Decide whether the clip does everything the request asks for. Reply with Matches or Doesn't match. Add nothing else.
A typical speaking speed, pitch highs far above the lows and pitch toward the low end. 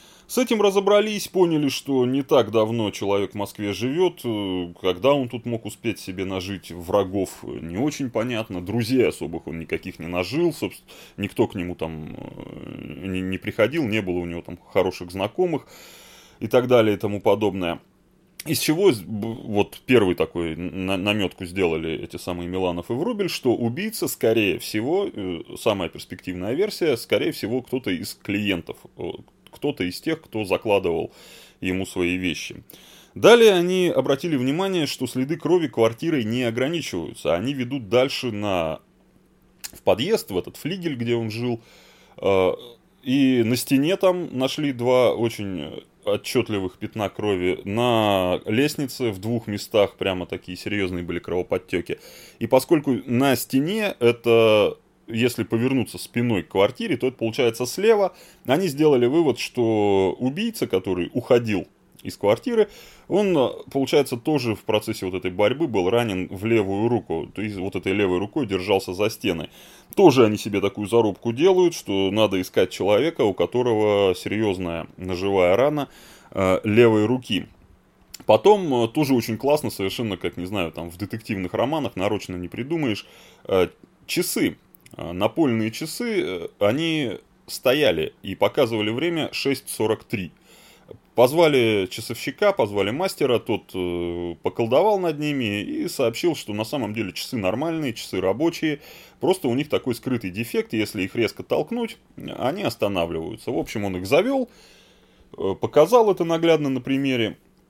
Matches